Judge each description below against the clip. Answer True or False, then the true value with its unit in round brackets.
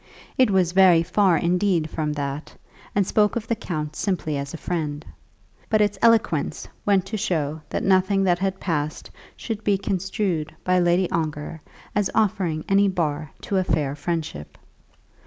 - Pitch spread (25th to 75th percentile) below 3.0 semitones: False (4.1 semitones)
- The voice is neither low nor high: True (180 Hz)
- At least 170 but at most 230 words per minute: False (160 wpm)